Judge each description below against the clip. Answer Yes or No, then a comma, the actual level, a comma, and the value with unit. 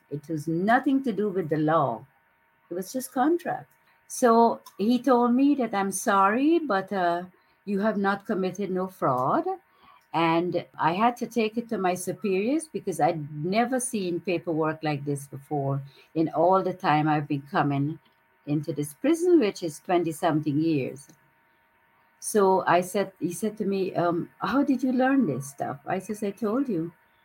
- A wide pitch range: Yes, wide, 6.3 semitones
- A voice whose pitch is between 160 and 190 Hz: Yes, medium, 185 Hz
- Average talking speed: Yes, average, 170 wpm